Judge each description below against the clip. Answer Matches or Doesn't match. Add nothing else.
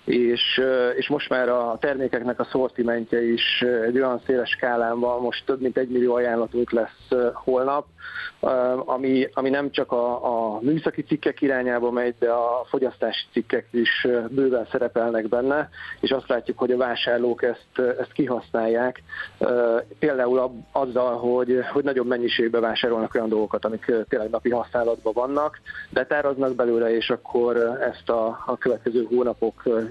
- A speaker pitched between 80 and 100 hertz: Doesn't match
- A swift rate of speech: Doesn't match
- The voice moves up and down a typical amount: Doesn't match